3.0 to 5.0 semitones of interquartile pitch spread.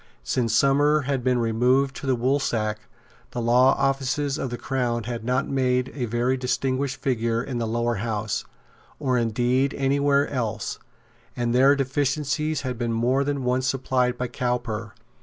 No: narrow, 2.4 semitones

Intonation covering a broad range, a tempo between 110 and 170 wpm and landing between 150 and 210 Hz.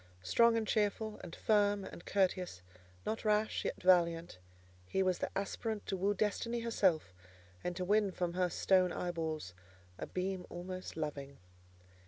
No: average, 3.2 semitones; average, 150 wpm; medium, 185 Hz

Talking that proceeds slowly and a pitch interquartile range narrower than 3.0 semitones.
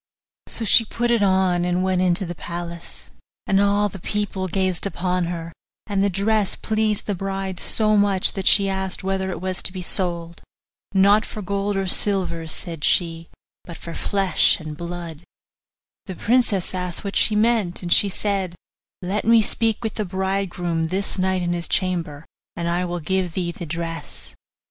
No: average, 175 wpm; narrow, 2.6 semitones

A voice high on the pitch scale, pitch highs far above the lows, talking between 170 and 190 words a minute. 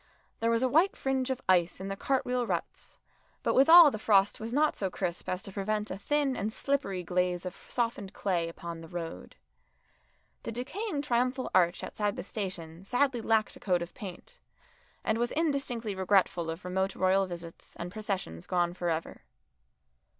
Yes: high, 200 Hz; wide, 5.7 semitones; average, 180 wpm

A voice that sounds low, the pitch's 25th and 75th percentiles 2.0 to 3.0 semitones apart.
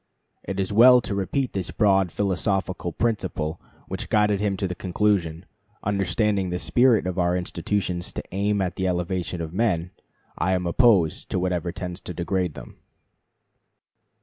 Yes: very low, 95 Hz; narrow, 2.6 semitones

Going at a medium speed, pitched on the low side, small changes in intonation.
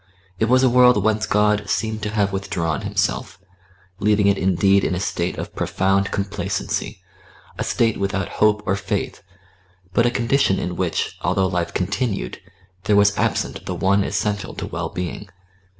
Yes: average, 165 wpm; low, 100 Hz; narrow, 1.9 semitones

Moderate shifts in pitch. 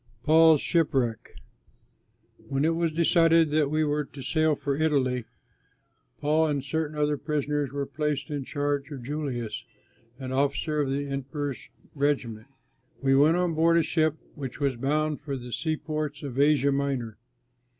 No: narrow, 2.1 semitones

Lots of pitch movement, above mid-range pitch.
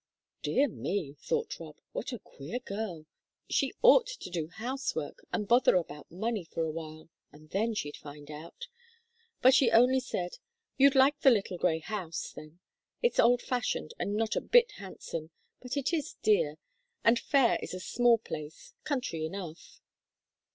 Yes: wide, 7.9 semitones; high, 210 Hz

